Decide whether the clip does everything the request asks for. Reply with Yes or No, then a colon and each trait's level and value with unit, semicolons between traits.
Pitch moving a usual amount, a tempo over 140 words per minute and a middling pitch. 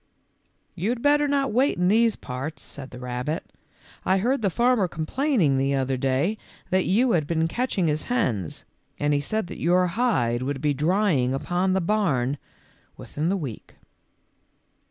No: wide, 7.9 semitones; average, 175 wpm; medium, 170 Hz